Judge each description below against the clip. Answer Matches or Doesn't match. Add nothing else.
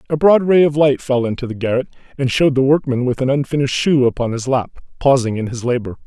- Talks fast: Matches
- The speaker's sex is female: Doesn't match